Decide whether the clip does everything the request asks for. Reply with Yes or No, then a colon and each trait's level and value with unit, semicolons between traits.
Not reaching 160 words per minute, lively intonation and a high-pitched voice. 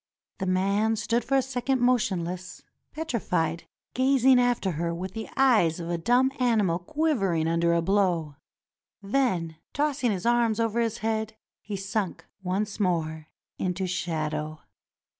Yes: average, 140 wpm; wide, 5.9 semitones; high, 200 Hz